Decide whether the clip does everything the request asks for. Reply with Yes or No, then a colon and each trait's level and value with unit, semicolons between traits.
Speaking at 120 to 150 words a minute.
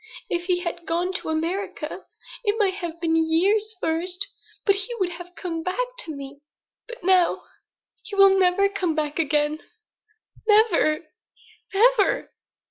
Yes: average, 140 wpm